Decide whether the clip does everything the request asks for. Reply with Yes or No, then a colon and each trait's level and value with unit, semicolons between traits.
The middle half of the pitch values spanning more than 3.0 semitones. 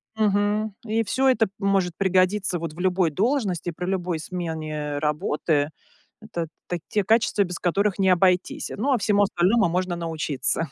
Yes: average, 3.5 semitones